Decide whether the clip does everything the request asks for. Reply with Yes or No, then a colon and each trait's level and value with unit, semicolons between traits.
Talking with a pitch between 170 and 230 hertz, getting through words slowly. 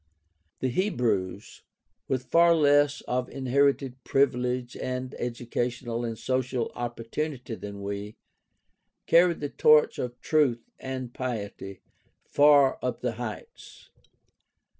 No: low, 125 Hz; slow, 110 wpm